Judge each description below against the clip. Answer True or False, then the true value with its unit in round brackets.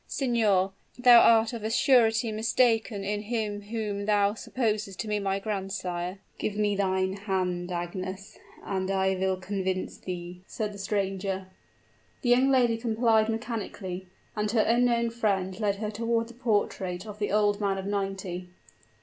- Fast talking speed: False (155 wpm)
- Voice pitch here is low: False (205 Hz)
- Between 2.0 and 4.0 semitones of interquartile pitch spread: True (2.8 semitones)